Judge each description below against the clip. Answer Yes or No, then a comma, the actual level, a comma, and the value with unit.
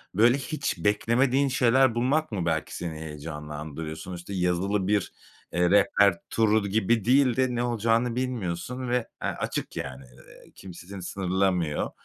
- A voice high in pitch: No, low, 100 Hz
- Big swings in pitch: Yes, wide, 5.8 semitones